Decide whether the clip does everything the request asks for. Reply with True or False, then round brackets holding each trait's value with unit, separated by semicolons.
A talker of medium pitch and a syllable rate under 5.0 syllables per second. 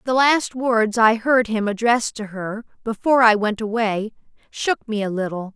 False (225 Hz; 4.5 syllables/s)